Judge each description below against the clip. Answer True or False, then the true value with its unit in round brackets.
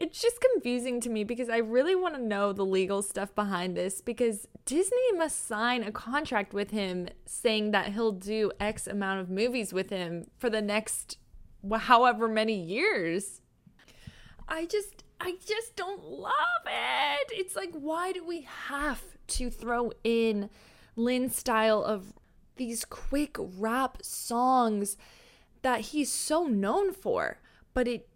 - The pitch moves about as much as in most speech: False (5.8 semitones)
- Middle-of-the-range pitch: False (235 Hz)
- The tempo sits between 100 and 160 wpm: True (150 wpm)